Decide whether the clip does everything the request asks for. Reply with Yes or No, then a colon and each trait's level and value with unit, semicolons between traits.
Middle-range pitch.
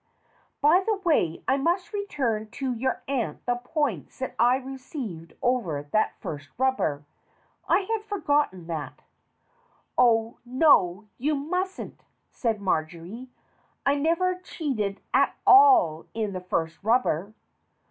No: very high, 250 Hz